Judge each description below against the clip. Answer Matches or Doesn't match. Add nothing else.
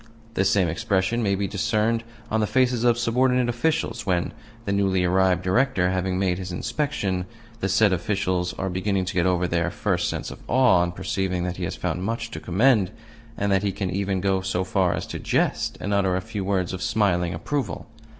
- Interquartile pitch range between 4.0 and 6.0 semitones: Doesn't match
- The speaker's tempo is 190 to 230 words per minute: Matches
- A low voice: Matches